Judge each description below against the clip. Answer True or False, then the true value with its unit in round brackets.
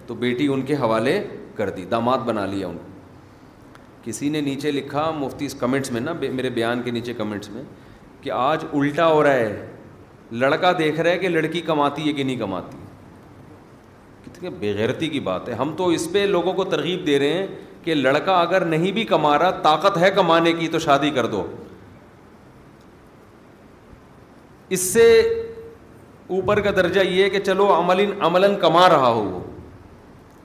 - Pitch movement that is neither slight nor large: False (6.9 semitones)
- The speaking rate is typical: True (170 wpm)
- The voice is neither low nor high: True (150 Hz)